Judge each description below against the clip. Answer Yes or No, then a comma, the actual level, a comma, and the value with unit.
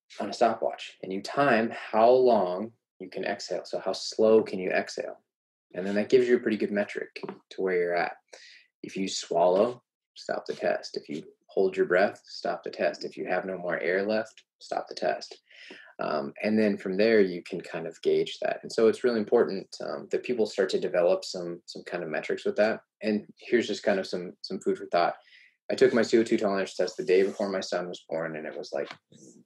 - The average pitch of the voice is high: Yes, very high, 370 Hz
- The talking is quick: Yes, fast, 225 wpm